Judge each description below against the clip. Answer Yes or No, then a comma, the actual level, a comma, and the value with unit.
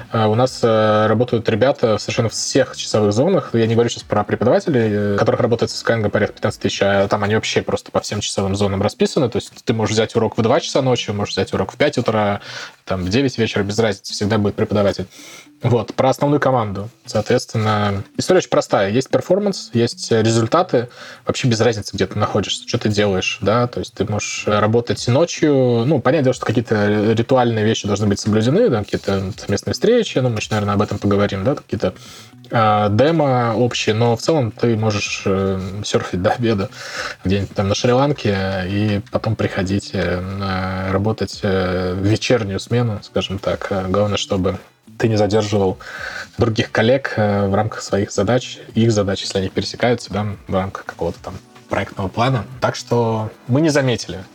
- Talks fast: Yes, fast, 175 wpm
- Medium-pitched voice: No, low, 110 Hz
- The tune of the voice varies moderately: Yes, average, 3.3 semitones